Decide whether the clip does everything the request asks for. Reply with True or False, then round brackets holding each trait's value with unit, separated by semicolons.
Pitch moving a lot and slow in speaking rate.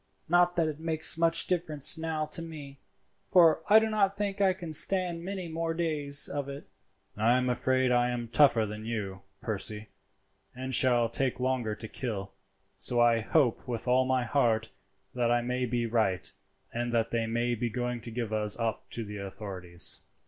False (5.7 semitones; 185 wpm)